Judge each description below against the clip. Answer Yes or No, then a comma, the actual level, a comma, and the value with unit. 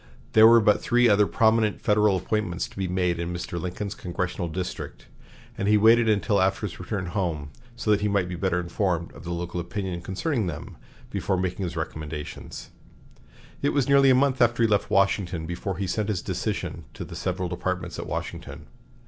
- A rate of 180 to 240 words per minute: Yes, average, 190 wpm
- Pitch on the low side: Yes, very low, 95 Hz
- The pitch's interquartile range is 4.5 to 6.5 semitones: No, average, 3.4 semitones